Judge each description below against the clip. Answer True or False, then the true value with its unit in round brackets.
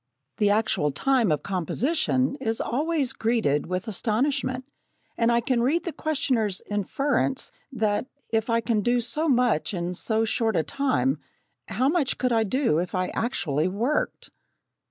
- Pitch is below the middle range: False (235 Hz)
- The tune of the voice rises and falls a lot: False (4.5 semitones)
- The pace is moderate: True (155 wpm)